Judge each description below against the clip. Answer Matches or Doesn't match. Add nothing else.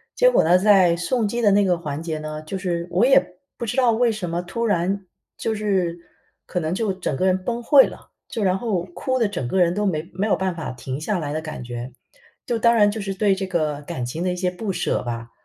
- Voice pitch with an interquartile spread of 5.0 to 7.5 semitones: Doesn't match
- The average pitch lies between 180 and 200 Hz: Matches